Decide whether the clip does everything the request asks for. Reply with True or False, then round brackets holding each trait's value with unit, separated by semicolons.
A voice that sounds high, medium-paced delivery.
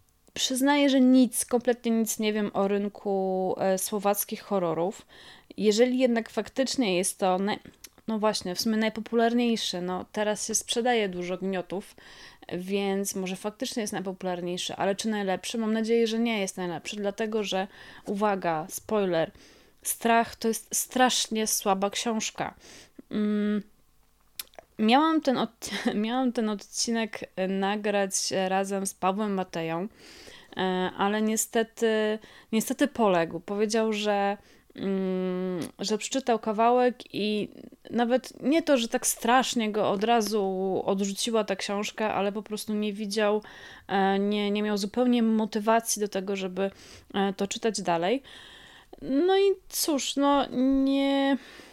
True (215 Hz; 125 wpm)